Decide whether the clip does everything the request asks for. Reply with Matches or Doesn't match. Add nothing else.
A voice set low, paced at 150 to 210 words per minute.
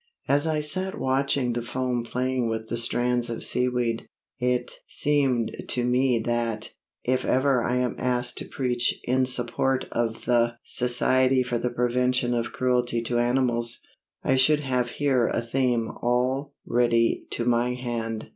Matches